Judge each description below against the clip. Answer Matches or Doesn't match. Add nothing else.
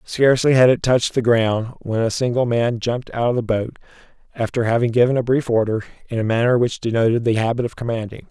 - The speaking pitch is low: Matches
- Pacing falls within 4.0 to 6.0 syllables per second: Doesn't match